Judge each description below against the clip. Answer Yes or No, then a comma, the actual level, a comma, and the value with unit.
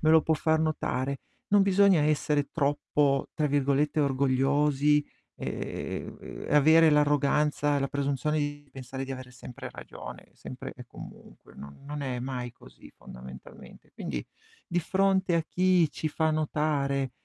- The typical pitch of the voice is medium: Yes, medium, 145 Hz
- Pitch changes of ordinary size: No, narrow, 2.3 semitones